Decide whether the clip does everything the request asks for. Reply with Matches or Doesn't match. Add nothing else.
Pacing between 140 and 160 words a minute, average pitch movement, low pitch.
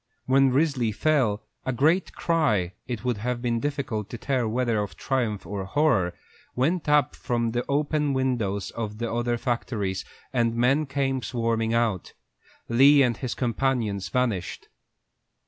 Matches